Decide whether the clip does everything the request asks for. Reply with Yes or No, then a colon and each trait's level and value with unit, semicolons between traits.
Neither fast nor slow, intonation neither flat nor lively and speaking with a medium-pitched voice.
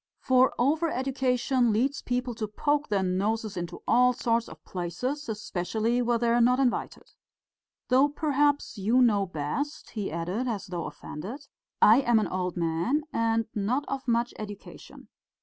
No: average, 155 wpm; average, 4.4 semitones; high, 235 Hz